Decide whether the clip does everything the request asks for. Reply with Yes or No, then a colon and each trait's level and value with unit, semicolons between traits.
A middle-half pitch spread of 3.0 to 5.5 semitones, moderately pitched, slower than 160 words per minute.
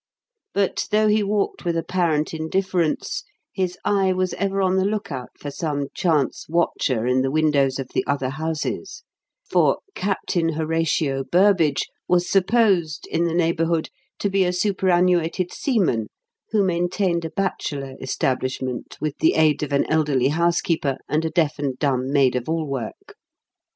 Yes: average, 4.5 semitones; medium, 165 Hz; average, 150 wpm